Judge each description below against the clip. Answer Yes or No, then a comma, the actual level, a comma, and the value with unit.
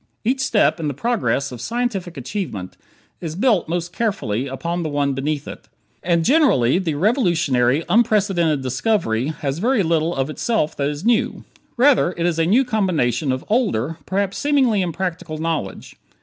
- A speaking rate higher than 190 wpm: No, average, 160 wpm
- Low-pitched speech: No, medium, 170 Hz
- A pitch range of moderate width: No, wide, 6.9 semitones